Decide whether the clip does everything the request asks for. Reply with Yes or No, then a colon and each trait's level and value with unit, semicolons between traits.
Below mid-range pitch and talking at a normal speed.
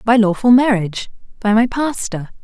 No: high, 220 Hz; average, 150 wpm